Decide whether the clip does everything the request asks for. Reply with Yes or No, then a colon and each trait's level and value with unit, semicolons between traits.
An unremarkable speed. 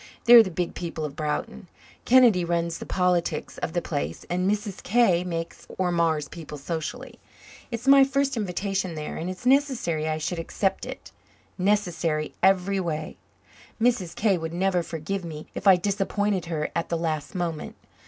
Yes: average, 165 wpm